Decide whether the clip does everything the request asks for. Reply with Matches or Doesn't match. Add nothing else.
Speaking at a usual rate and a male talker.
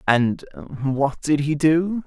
Matches